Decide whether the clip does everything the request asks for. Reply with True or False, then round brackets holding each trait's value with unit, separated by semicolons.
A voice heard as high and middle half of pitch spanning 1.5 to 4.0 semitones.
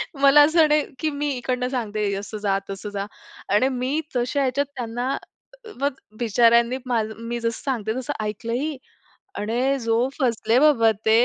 True (240 Hz; 3.7 semitones)